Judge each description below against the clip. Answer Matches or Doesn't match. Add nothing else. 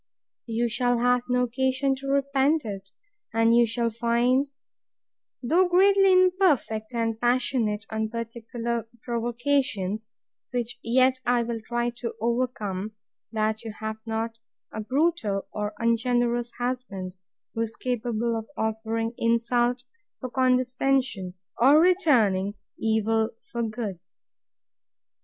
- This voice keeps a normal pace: Doesn't match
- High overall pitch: Matches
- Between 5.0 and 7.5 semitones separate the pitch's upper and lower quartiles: Doesn't match